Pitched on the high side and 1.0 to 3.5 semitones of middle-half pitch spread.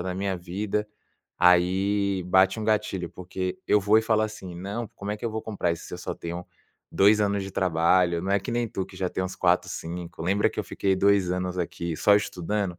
No: very low, 95 Hz; narrow, 2.4 semitones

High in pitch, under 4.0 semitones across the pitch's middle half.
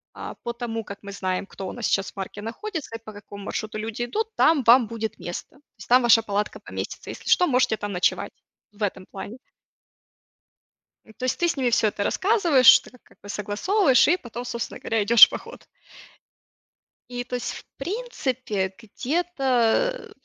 No: high, 235 Hz; average, 4.3 semitones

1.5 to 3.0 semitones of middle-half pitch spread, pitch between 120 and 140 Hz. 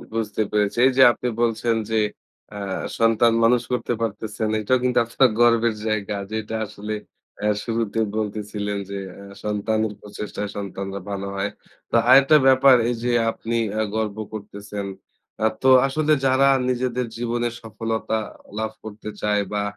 No: narrow, 2.4 semitones; low, 110 Hz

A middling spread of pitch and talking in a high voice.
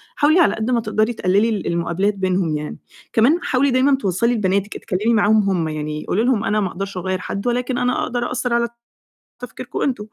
Yes: average, 4.7 semitones; high, 215 Hz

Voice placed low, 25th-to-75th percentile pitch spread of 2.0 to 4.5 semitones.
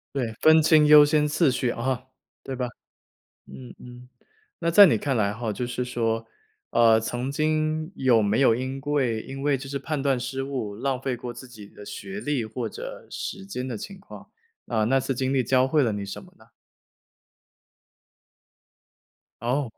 Yes: low, 130 Hz; average, 3.4 semitones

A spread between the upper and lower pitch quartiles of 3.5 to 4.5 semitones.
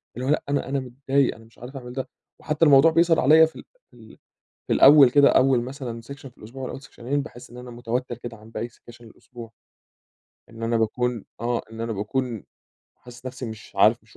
No: average, 2.8 semitones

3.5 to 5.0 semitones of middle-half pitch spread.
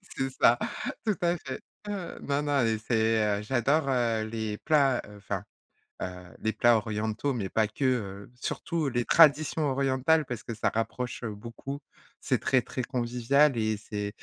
Yes: average, 4.0 semitones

